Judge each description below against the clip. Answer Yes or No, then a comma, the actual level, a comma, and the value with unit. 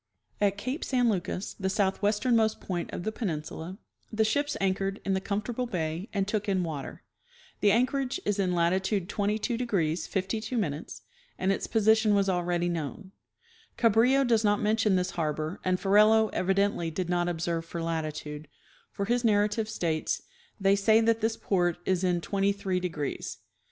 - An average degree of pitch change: Yes, average, 3.7 semitones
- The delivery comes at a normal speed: Yes, average, 160 wpm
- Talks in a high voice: Yes, high, 195 Hz